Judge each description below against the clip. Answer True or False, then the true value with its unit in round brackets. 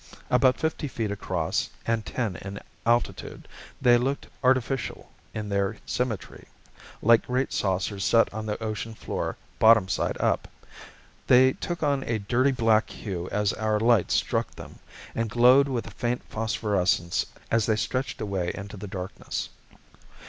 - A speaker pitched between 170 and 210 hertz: False (110 Hz)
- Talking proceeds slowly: False (150 wpm)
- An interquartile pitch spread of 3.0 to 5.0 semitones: True (3.6 semitones)